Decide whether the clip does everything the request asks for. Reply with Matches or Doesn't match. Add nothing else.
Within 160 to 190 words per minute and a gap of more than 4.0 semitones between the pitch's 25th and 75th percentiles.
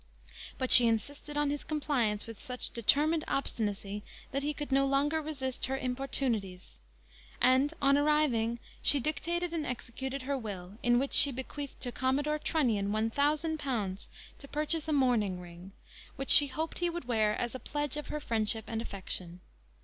Matches